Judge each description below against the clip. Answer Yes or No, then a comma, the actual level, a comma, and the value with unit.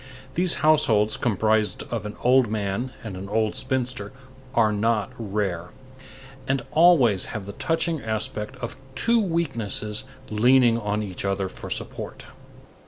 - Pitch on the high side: No, low, 110 Hz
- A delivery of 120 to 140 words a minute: Yes, slow, 135 wpm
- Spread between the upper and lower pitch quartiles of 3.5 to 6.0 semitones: Yes, average, 4.0 semitones